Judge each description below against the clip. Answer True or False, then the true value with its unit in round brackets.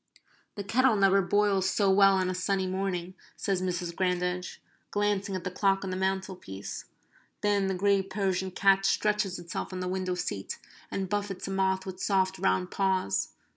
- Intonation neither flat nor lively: False (1.3 semitones)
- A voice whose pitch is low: False (190 Hz)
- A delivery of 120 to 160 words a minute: False (175 wpm)